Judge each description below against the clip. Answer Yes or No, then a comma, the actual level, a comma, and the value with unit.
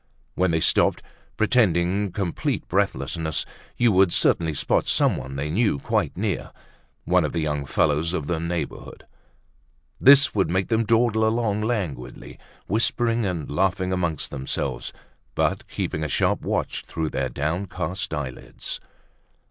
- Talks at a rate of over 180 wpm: No, slow, 135 wpm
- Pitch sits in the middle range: No, very low, 85 Hz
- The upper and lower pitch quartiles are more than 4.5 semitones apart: Yes, average, 5.3 semitones